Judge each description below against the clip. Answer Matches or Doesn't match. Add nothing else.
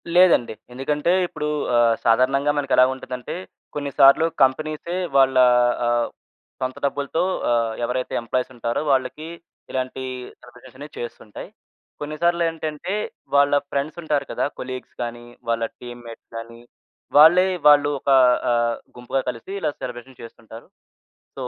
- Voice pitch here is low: Matches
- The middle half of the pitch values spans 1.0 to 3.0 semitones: Doesn't match